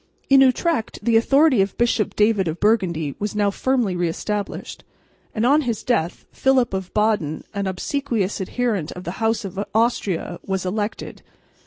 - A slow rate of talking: No, average, 160 wpm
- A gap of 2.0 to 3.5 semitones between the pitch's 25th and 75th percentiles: No, average, 4.1 semitones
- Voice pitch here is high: Yes, high, 210 Hz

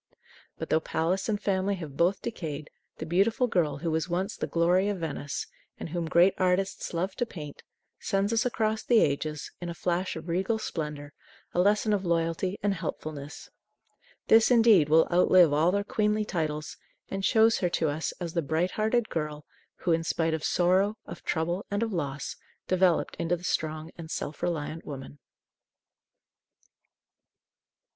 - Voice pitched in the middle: Yes, medium, 175 Hz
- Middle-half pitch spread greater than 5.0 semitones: No, average, 3.8 semitones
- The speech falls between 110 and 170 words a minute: Yes, average, 165 wpm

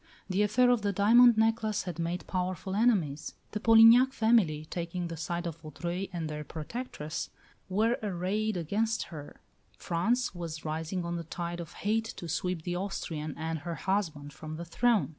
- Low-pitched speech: No, medium, 180 Hz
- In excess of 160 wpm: Yes, average, 170 wpm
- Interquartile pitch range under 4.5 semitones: No, average, 4.9 semitones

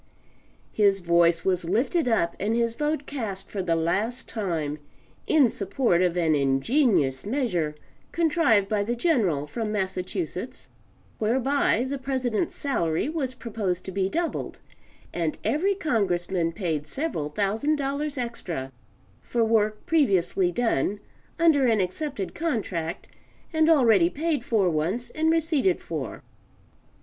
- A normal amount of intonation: No, wide, 7.8 semitones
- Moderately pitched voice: No, high, 220 Hz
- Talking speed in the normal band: No, slow, 130 wpm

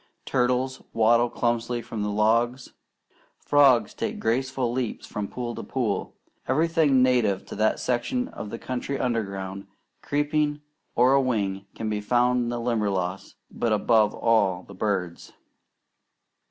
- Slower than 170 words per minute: Yes, average, 140 wpm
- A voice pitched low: Yes, low, 120 Hz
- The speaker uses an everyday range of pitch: Yes, average, 3.5 semitones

